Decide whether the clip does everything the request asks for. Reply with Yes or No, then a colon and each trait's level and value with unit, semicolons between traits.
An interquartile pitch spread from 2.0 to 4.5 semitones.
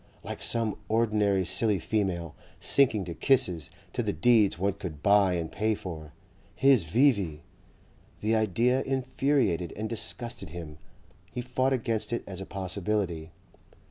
No: average, 5.0 semitones